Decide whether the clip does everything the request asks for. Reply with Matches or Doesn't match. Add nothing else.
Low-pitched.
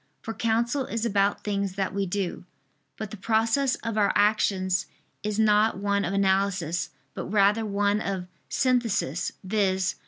Doesn't match